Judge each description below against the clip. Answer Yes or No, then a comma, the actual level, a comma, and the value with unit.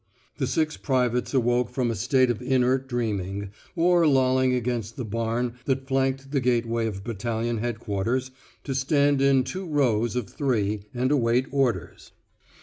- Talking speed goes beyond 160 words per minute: No, average, 150 wpm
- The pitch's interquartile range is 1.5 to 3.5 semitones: Yes, narrow, 2.6 semitones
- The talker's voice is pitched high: No, low, 125 Hz